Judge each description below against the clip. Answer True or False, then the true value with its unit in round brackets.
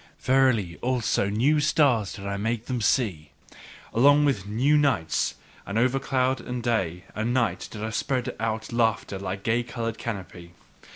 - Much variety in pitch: False (4.2 semitones)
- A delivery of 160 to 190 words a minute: True (165 wpm)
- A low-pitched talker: True (115 Hz)